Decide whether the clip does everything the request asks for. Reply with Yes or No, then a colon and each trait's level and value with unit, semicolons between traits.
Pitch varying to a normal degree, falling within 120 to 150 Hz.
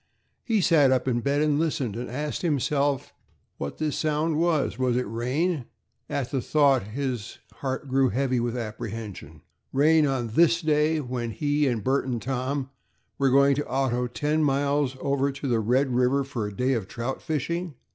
Yes: average, 3.1 semitones; low, 135 Hz